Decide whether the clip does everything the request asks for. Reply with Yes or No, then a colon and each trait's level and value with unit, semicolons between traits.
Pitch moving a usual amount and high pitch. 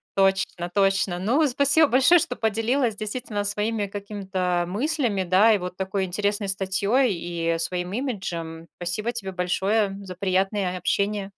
Yes: average, 3.3 semitones; high, 200 Hz